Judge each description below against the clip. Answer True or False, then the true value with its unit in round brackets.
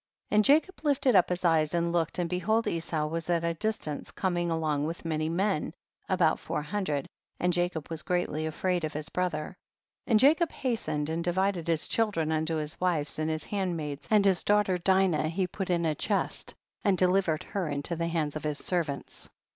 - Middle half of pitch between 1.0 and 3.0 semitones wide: False (3.4 semitones)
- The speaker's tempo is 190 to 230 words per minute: True (205 wpm)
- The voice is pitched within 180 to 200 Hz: False (170 Hz)